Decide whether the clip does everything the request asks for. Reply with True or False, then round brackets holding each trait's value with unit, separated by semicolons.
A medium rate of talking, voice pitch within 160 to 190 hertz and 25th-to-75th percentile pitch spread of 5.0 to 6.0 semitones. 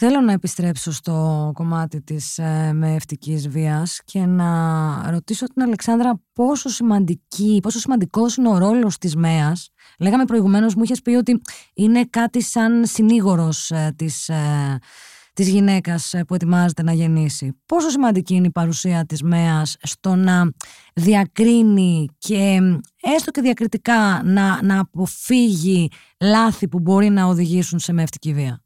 True (135 wpm; 185 Hz; 5.4 semitones)